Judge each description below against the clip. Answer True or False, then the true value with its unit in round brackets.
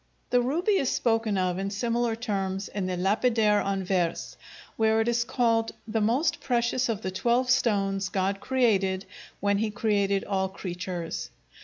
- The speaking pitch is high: True (210 Hz)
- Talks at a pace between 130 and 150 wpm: False (160 wpm)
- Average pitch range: True (3.6 semitones)